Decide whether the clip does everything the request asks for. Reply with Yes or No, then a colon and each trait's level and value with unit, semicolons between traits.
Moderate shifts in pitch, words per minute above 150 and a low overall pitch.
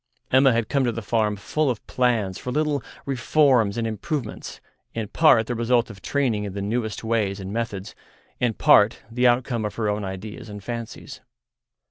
Yes: average, 3.2 semitones; average, 180 wpm; low, 115 Hz